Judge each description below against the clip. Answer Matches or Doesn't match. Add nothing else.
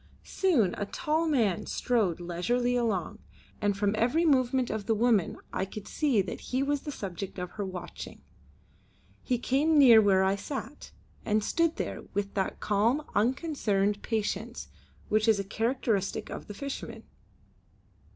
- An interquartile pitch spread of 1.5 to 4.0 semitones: Doesn't match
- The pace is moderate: Matches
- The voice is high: Matches